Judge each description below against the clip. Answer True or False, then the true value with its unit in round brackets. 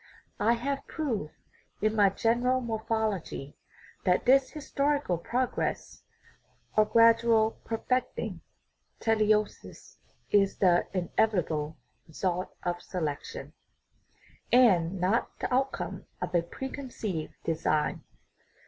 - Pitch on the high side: True (215 Hz)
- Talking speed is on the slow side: True (95 wpm)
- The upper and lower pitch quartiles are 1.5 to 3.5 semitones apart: False (5.3 semitones)